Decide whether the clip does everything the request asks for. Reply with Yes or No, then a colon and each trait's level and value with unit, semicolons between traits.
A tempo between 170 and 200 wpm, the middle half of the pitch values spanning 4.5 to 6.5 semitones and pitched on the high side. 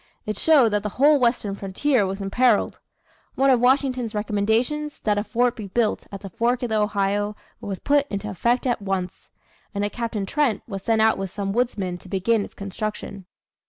No: average, 195 wpm; average, 3.7 semitones; high, 215 Hz